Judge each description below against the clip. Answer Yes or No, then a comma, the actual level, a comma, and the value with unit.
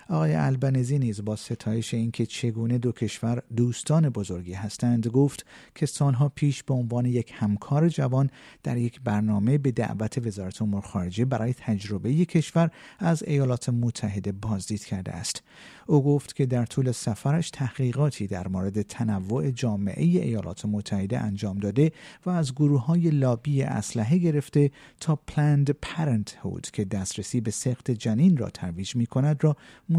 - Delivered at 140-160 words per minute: Yes, average, 150 wpm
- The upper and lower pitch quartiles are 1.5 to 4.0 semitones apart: No, average, 5.1 semitones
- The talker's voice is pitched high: No, low, 120 Hz